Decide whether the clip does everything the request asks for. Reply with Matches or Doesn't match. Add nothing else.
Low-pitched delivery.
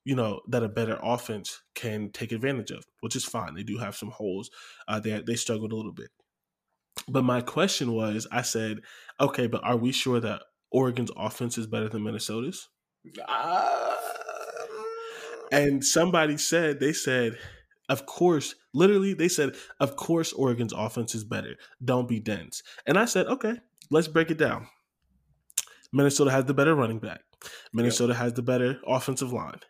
Matches